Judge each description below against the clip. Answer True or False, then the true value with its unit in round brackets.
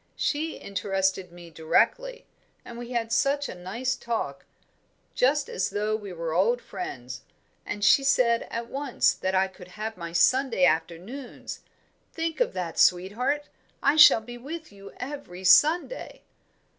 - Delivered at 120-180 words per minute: True (145 wpm)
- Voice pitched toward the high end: True (220 Hz)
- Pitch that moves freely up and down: True (7.0 semitones)